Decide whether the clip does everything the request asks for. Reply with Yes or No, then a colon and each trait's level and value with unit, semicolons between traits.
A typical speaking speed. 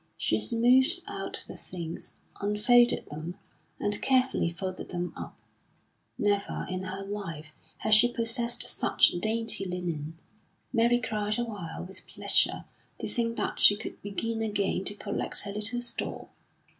Yes: average, 145 wpm